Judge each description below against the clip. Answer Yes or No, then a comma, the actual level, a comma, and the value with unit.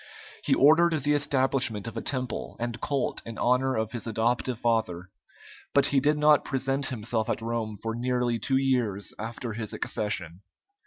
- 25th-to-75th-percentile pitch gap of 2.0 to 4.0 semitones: Yes, average, 3.2 semitones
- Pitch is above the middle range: No, low, 120 Hz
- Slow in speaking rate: No, average, 165 wpm